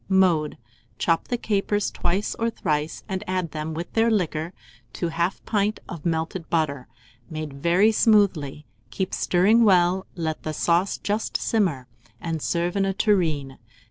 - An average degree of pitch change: Yes, average, 4.1 semitones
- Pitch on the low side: No, medium, 175 Hz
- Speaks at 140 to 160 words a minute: Yes, average, 150 wpm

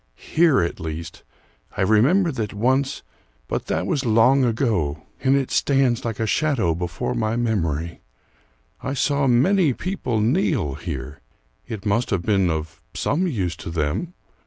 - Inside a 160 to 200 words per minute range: No, average, 150 wpm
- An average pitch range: No, wide, 7.9 semitones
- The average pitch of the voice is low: Yes, low, 115 Hz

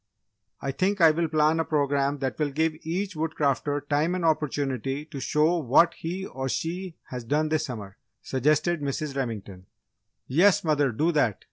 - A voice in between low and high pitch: Yes, medium, 150 Hz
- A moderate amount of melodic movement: Yes, average, 3.2 semitones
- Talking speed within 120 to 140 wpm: No, average, 165 wpm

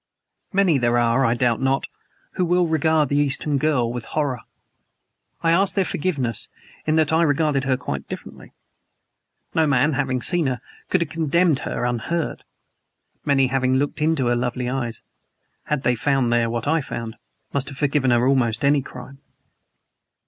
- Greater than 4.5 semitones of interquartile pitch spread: No, average, 4.1 semitones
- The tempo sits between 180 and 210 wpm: No, average, 165 wpm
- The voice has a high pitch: No, low, 135 Hz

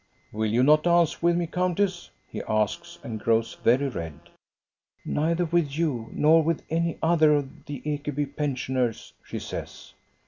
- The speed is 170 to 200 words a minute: No, average, 150 wpm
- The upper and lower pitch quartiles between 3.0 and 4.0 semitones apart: No, average, 5.1 semitones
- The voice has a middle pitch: Yes, medium, 150 Hz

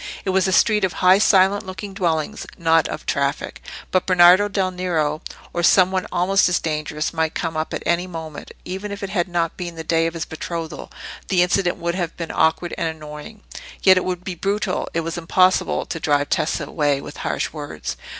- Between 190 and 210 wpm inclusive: Yes, average, 200 wpm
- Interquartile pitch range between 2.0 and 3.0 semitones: Yes, narrow, 2.6 semitones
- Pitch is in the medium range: Yes, medium, 175 Hz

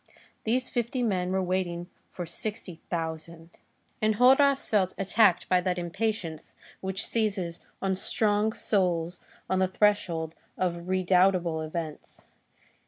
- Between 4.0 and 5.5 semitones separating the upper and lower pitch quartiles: No, average, 3.6 semitones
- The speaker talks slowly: Yes, slow, 115 wpm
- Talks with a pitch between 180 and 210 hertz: Yes, medium, 185 Hz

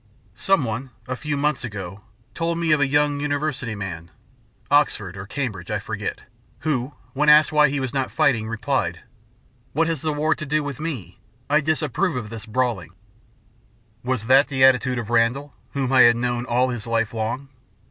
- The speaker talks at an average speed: Yes, average, 180 wpm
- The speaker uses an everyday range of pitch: Yes, average, 4.3 semitones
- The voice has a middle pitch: No, low, 130 Hz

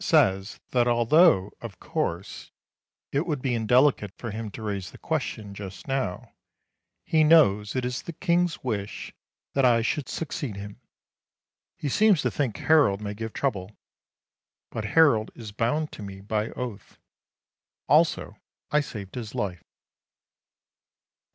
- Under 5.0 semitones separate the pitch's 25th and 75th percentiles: No, wide, 5.6 semitones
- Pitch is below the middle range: Yes, low, 115 Hz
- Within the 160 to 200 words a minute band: No, average, 140 wpm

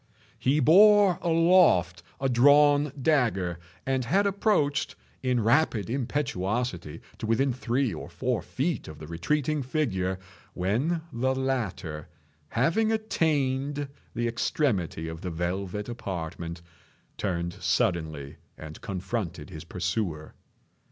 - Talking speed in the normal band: No, slow, 110 wpm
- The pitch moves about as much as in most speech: No, wide, 8.2 semitones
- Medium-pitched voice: No, low, 120 Hz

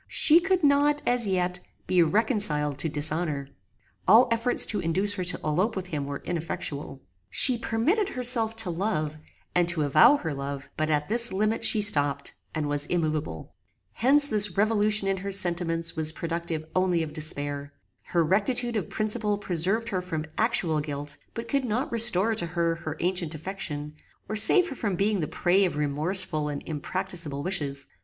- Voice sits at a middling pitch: Yes, medium, 180 Hz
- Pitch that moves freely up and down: Yes, wide, 5.9 semitones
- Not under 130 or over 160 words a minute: No, average, 170 wpm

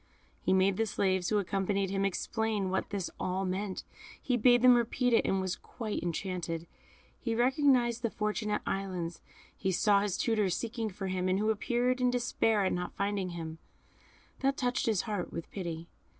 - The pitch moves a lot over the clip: No, average, 3.7 semitones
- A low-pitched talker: No, high, 200 Hz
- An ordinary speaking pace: Yes, average, 180 wpm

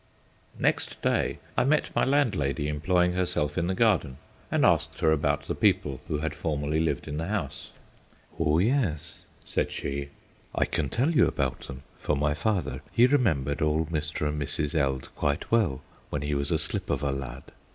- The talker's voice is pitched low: Yes, very low, 75 Hz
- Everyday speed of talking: Yes, average, 185 wpm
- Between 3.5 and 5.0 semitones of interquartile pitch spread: Yes, average, 4.0 semitones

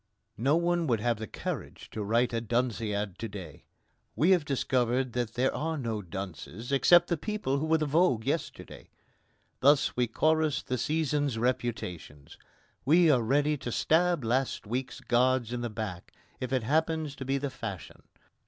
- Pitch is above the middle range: No, low, 130 Hz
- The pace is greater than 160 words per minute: Yes, average, 170 wpm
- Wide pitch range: No, average, 4.9 semitones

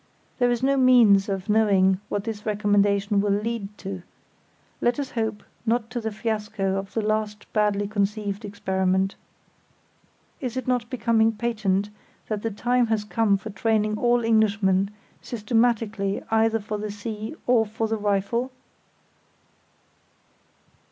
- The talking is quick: No, average, 140 wpm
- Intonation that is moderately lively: No, narrow, 2.1 semitones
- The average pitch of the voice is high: Yes, high, 215 Hz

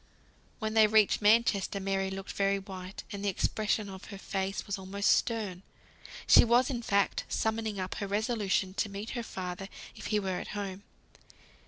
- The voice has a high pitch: Yes, high, 200 Hz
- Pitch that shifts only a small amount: Yes, narrow, 2.1 semitones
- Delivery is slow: No, average, 175 wpm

